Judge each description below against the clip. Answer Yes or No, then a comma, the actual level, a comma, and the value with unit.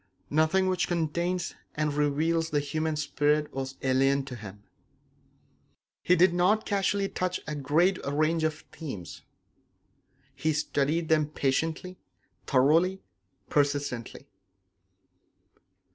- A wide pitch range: No, average, 3.4 semitones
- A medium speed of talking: No, slow, 105 wpm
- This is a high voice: No, medium, 155 Hz